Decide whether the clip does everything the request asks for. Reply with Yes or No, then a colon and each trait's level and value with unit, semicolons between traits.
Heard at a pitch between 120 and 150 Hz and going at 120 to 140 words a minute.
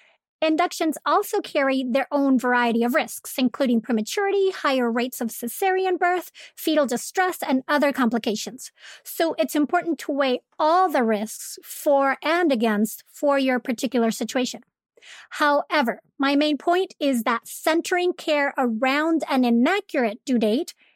No: very high, 280 Hz; slow, 135 wpm